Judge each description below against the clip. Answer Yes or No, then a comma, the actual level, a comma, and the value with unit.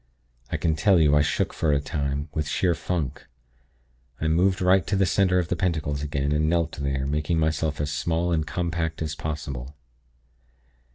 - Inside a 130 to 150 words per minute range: No, average, 180 wpm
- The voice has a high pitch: No, very low, 80 Hz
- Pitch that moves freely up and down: No, average, 2.9 semitones